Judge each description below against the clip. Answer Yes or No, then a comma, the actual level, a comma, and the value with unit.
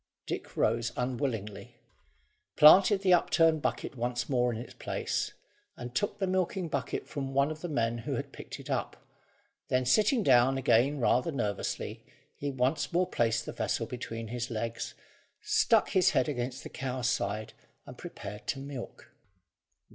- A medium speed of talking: Yes, average, 160 wpm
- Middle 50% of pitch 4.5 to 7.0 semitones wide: Yes, average, 4.9 semitones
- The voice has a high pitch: No, low, 130 Hz